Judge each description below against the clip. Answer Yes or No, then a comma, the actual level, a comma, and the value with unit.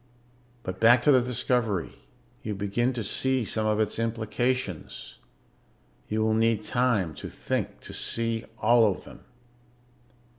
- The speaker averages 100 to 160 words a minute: Yes, average, 140 wpm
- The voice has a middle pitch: No, low, 115 Hz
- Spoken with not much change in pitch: Yes, narrow, 2.3 semitones